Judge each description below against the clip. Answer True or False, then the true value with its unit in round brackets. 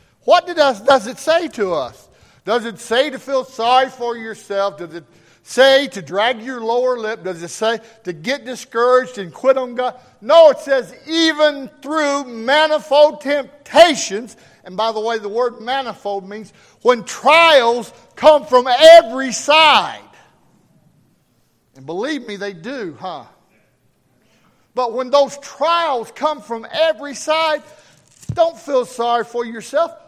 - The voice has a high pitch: True (255 Hz)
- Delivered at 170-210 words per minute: False (145 wpm)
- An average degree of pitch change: True (4.7 semitones)